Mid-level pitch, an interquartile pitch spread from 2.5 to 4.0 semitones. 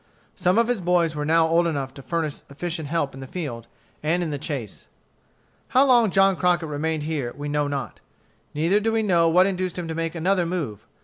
Yes: medium, 165 Hz; average, 3.6 semitones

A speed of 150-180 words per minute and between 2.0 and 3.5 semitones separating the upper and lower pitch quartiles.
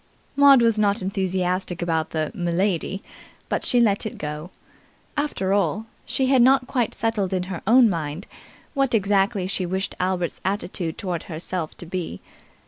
No: average, 155 wpm; average, 4.1 semitones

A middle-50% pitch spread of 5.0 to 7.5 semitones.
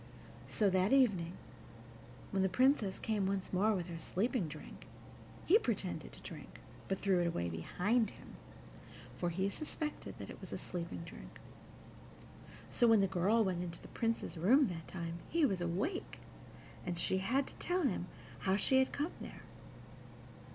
Yes: wide, 5.4 semitones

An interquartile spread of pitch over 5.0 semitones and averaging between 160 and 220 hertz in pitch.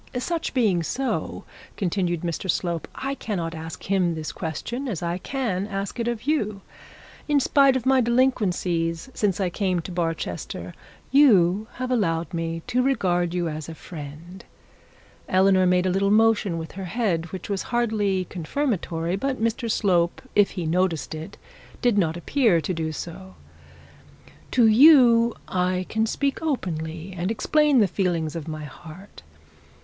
Yes: wide, 5.5 semitones; high, 190 Hz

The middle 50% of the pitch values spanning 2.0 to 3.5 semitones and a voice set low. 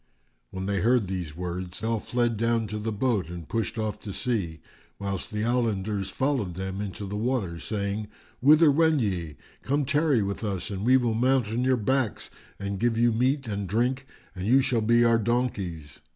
No: average, 4.0 semitones; low, 110 Hz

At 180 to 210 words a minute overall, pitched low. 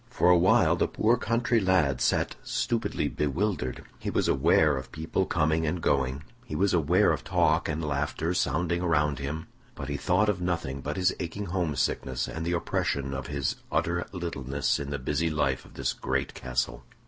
Yes: average, 185 wpm; very low, 80 Hz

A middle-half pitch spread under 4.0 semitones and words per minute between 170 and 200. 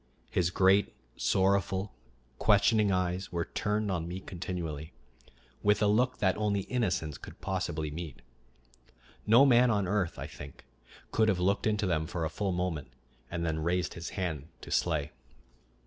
No: average, 3.5 semitones; average, 155 wpm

